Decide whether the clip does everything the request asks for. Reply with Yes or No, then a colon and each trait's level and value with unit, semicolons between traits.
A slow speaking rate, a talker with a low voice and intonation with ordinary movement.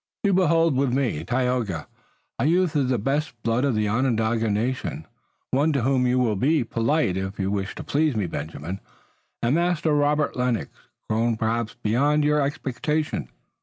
No: average, 165 wpm; low, 125 Hz; average, 5.0 semitones